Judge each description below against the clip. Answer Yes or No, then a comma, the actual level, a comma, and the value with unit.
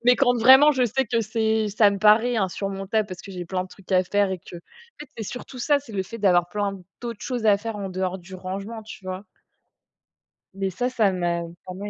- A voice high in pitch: Yes, high, 205 Hz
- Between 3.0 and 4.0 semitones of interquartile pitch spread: Yes, average, 3.6 semitones